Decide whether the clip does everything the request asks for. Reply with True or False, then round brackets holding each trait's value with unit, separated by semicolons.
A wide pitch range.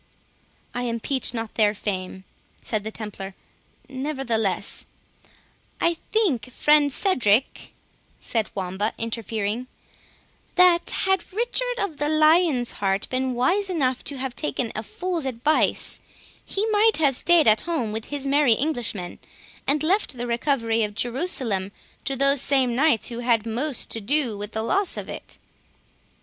True (5.7 semitones)